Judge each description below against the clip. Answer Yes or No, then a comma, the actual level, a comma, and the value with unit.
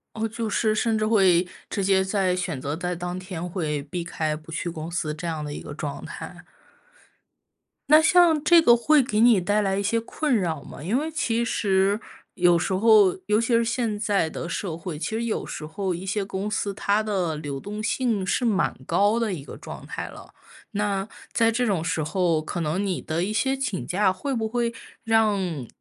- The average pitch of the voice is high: Yes, high, 195 Hz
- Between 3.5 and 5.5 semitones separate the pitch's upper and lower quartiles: Yes, average, 4.6 semitones